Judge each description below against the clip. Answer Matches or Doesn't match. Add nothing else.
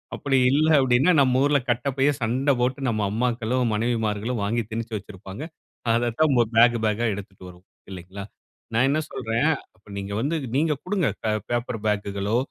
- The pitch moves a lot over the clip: Doesn't match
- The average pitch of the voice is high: Doesn't match